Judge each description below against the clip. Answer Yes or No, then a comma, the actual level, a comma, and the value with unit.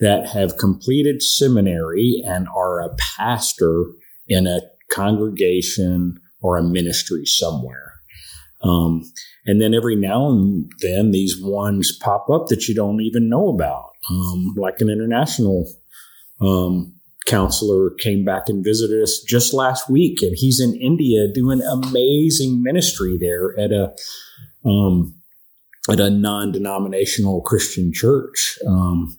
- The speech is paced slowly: Yes, slow, 130 wpm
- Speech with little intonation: No, average, 3.7 semitones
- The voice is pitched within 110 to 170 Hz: No, low, 100 Hz